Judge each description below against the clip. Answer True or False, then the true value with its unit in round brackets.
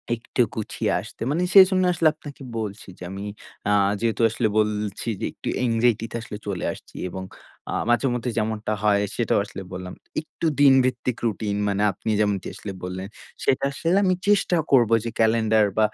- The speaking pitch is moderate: False (110 Hz)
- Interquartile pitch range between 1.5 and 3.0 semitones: False (3.7 semitones)